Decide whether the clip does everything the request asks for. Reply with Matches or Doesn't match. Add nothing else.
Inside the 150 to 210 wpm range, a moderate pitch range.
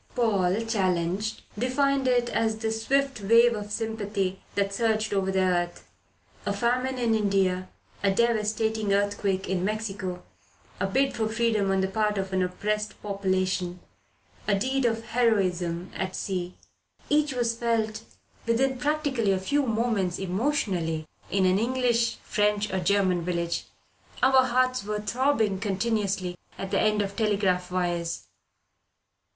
Doesn't match